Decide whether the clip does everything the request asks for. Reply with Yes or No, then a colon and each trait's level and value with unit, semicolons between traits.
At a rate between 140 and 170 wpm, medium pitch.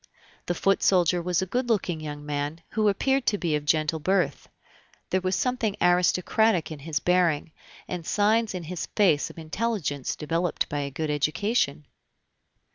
Yes: average, 165 wpm; medium, 175 Hz